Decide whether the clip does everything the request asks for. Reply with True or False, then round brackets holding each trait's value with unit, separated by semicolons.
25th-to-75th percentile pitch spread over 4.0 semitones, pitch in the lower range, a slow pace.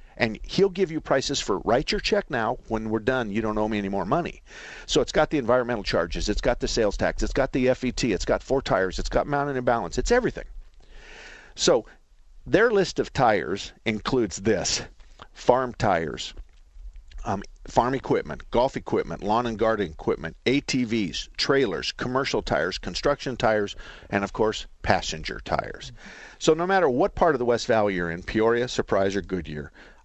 False (5.0 semitones; 115 Hz; 180 wpm)